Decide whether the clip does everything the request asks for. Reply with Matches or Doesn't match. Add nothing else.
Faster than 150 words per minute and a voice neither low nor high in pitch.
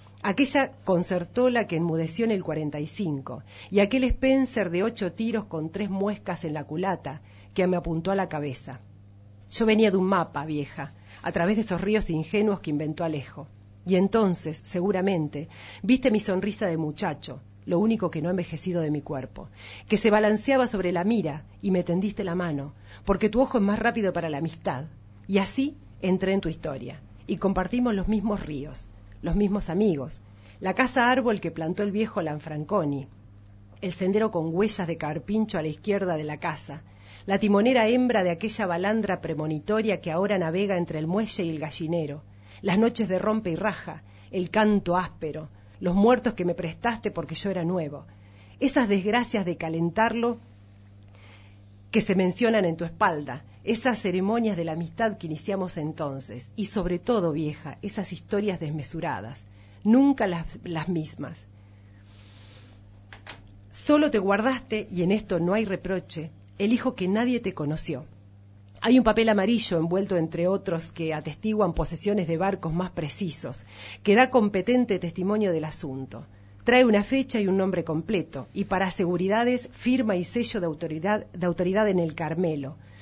Matches